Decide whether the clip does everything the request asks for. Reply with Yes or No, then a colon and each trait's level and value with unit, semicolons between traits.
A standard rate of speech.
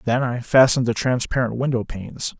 Yes: average, 175 wpm